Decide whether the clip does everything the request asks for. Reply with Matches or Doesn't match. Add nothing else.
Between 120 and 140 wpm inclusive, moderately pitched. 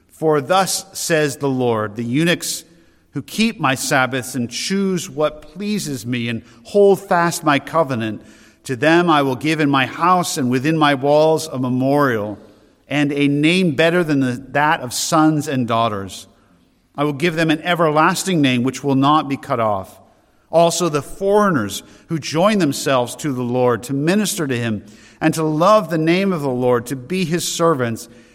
Doesn't match